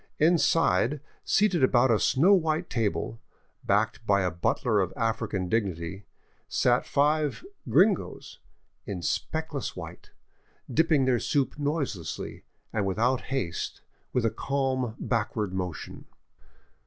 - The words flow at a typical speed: No, slow, 120 wpm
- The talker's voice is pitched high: No, low, 125 Hz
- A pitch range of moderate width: No, wide, 6.8 semitones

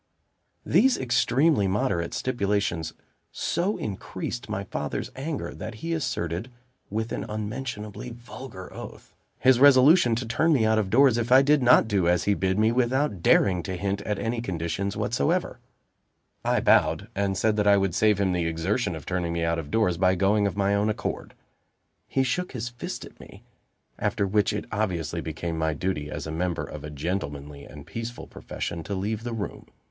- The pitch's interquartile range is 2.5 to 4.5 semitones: No, average, 5.3 semitones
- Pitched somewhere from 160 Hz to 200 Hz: No, low, 100 Hz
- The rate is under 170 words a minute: No, average, 185 wpm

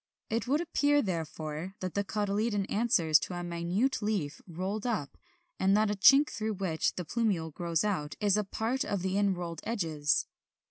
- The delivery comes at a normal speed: Yes, average, 175 wpm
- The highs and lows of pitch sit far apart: No, average, 4.2 semitones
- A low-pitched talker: No, high, 195 Hz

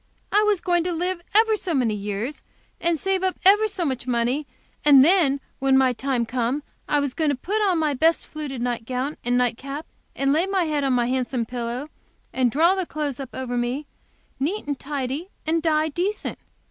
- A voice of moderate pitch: No, very high, 285 Hz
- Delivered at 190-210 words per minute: Yes, average, 200 wpm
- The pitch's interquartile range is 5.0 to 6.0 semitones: Yes, average, 5.3 semitones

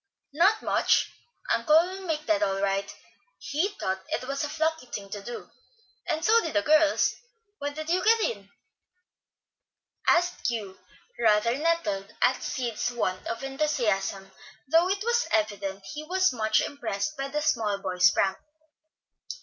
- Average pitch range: No, wide, 7.9 semitones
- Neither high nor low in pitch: No, very high, 270 Hz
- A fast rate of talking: No, average, 150 wpm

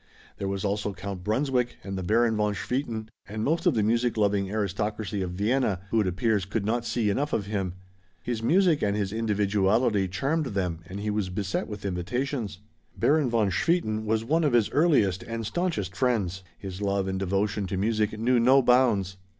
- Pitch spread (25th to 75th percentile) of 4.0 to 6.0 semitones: No, average, 3.4 semitones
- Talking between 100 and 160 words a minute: No, average, 190 wpm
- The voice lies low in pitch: Yes, low, 105 Hz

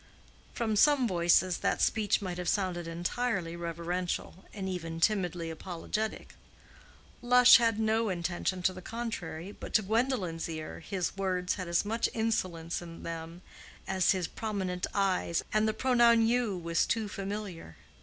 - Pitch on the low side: No, medium, 185 Hz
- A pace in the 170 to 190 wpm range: No, average, 145 wpm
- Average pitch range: Yes, average, 4.2 semitones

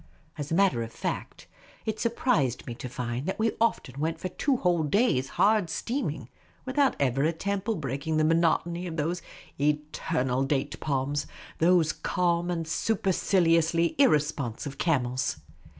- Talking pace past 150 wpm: No, average, 145 wpm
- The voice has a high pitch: No, medium, 160 Hz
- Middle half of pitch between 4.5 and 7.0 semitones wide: Yes, average, 4.9 semitones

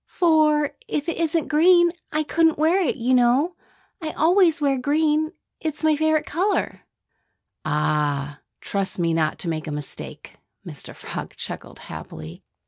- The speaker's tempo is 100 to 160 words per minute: Yes, average, 145 wpm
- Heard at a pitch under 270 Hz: No, very high, 300 Hz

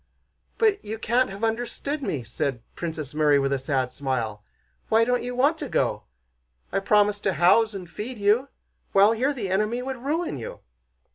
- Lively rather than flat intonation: Yes, wide, 8.4 semitones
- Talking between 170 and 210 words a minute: Yes, average, 180 wpm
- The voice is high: Yes, high, 210 Hz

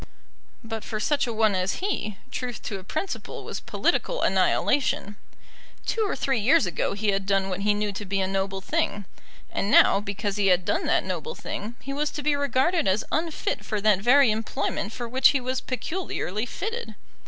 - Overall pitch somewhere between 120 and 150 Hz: No, high, 220 Hz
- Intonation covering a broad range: Yes, wide, 5.9 semitones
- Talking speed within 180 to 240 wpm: Yes, average, 195 wpm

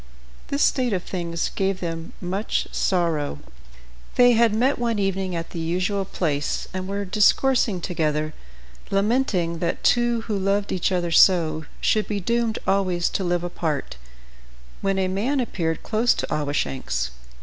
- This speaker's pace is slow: No, average, 150 wpm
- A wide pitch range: No, average, 4.2 semitones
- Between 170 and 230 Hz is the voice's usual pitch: Yes, medium, 185 Hz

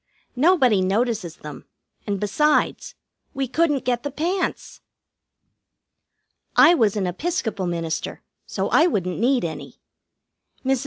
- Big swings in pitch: Yes, wide, 7.7 semitones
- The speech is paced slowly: Yes, slow, 115 wpm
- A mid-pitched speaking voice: No, high, 235 Hz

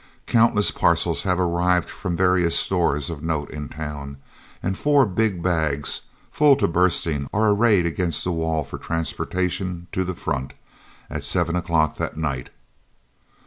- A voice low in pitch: Yes, very low, 85 Hz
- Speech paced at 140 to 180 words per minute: Yes, average, 145 wpm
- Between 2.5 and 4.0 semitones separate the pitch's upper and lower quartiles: Yes, average, 2.8 semitones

